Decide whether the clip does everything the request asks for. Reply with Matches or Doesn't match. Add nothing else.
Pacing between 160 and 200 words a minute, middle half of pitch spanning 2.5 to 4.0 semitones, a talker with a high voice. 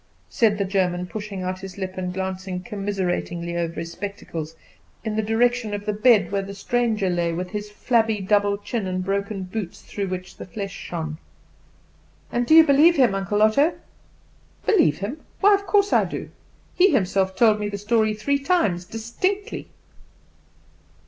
Matches